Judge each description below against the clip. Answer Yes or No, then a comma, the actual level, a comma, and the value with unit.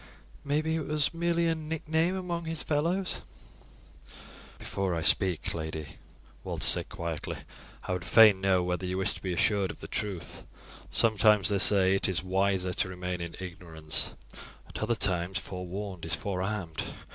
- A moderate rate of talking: Yes, average, 155 wpm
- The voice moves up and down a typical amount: No, wide, 8.2 semitones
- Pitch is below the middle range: Yes, very low, 95 Hz